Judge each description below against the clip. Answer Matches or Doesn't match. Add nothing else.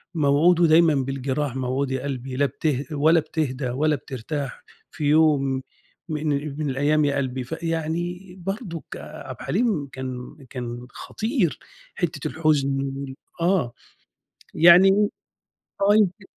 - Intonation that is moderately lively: Matches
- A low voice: Doesn't match